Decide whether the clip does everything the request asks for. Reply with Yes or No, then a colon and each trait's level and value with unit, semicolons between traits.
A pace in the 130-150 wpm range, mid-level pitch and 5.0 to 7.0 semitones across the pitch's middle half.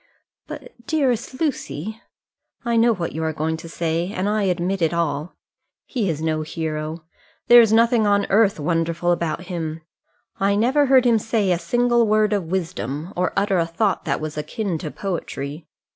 No: average, 180 wpm; medium, 180 Hz; average, 5.3 semitones